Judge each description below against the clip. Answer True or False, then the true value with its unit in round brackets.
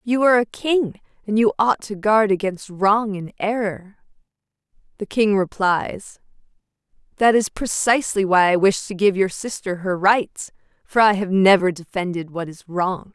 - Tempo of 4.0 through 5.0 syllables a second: True (4.5 syllables/s)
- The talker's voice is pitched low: False (200 Hz)